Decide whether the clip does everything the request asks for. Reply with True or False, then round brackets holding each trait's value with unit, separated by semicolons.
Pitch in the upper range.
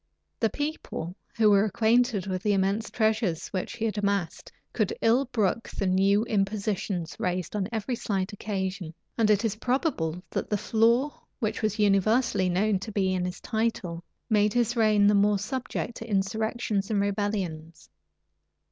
True (205 Hz)